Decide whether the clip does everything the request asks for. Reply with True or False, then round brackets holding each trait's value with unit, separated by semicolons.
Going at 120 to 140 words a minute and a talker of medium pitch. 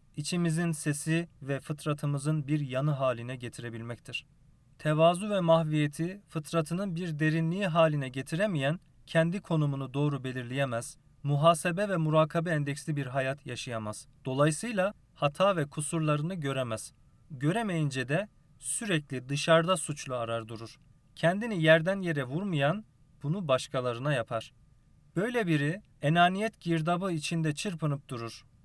False (110 wpm; 150 Hz)